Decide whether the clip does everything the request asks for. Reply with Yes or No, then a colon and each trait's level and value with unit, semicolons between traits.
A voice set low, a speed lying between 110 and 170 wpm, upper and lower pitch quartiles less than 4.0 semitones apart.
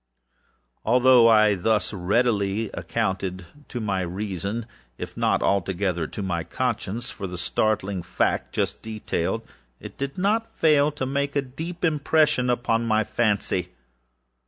No: low, 110 Hz; average, 140 wpm; average, 5.1 semitones